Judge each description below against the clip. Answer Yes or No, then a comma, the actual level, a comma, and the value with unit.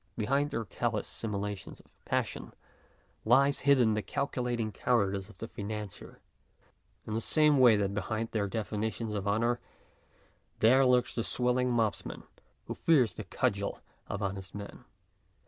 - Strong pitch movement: No, average, 3.2 semitones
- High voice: No, low, 110 Hz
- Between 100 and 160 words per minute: Yes, average, 140 wpm